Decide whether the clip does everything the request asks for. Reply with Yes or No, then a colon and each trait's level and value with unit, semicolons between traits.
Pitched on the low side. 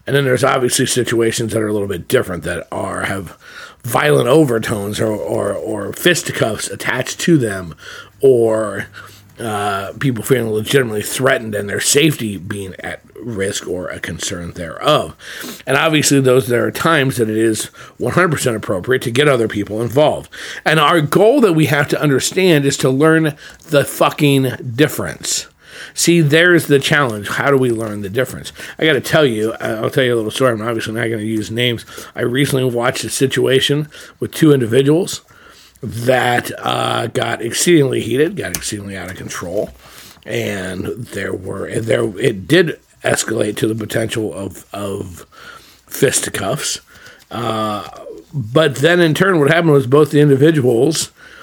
Yes: low, 125 Hz